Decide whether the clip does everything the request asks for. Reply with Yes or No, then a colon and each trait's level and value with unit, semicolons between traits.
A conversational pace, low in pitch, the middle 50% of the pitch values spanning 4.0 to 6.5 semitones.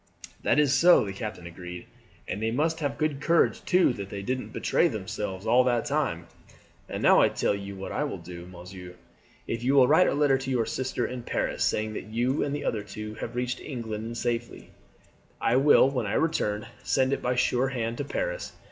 No: fast, 210 wpm; low, 120 Hz; average, 4.8 semitones